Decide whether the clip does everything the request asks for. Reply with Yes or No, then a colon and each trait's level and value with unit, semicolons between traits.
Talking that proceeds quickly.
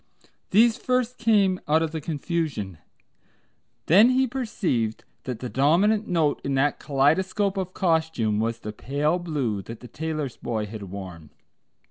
No: average, 145 wpm